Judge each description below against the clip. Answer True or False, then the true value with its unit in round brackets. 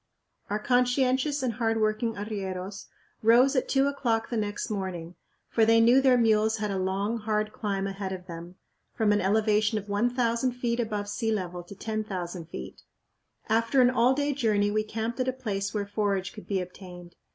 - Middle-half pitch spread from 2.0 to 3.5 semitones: True (3.0 semitones)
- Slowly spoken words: False (185 wpm)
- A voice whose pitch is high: True (215 Hz)